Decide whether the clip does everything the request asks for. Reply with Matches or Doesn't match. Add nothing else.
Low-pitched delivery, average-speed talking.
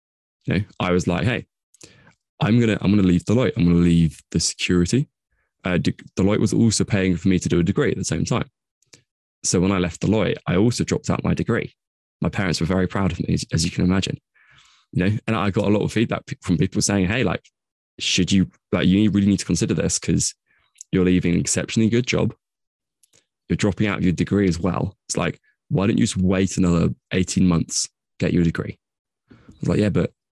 Doesn't match